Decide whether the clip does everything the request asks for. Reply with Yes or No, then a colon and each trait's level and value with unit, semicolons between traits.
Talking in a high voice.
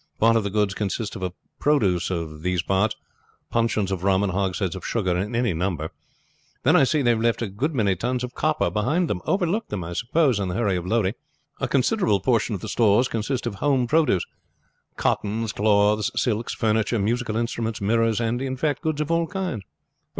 No: low, 110 Hz